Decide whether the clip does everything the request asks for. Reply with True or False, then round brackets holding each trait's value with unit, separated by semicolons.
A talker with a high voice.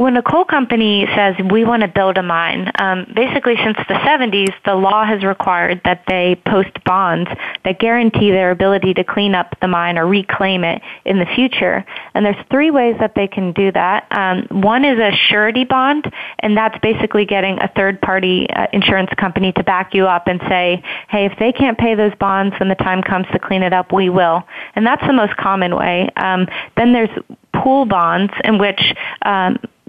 True (195 Hz)